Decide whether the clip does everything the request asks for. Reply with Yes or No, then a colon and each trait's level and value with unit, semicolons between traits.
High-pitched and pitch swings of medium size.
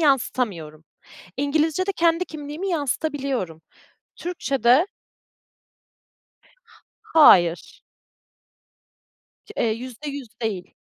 No: very high, 275 Hz; wide, 6.0 semitones